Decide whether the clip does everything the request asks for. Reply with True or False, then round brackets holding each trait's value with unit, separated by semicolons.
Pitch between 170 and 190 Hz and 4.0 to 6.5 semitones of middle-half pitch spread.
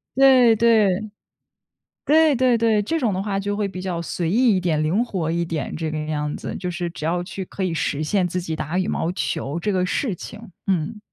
True (185 Hz; 4.7 semitones)